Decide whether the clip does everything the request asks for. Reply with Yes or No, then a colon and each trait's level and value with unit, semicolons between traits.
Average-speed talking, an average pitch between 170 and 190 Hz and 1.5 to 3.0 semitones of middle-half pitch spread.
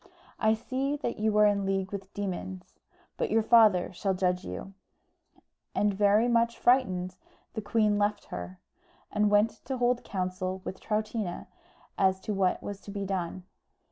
No: average, 160 wpm; high, 205 Hz; narrow, 2.6 semitones